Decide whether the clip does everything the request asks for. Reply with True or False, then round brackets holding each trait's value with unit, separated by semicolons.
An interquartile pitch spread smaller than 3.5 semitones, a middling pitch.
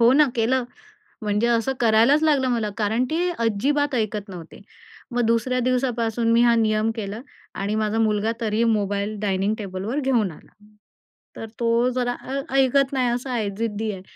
False (3.1 semitones; 230 Hz)